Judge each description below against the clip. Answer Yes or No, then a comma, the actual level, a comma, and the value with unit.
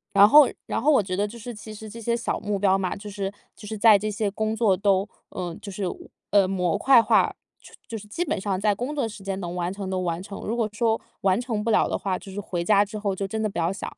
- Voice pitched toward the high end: Yes, high, 205 Hz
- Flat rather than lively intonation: Yes, narrow, 2.3 semitones